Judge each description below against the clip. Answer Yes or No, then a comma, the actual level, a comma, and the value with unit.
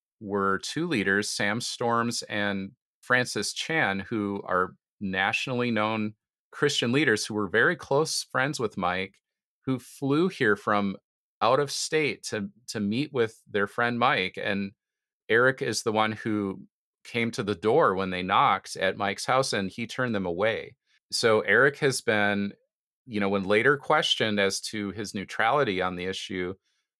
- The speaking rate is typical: Yes, average, 160 wpm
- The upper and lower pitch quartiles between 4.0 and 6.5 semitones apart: No, average, 3.1 semitones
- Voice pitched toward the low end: Yes, low, 105 Hz